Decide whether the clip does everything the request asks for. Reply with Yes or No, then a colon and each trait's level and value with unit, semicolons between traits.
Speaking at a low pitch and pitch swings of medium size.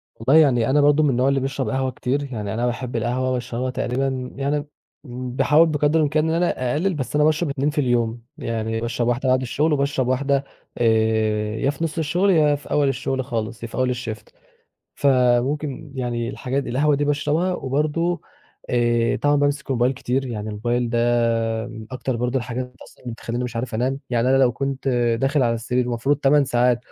Yes: low, 130 Hz; average, 3.0 semitones